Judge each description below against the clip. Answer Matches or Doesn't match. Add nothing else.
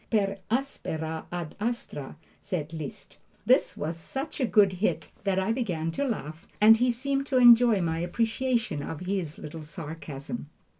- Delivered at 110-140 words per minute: Doesn't match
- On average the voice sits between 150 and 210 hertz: Matches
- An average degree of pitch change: Doesn't match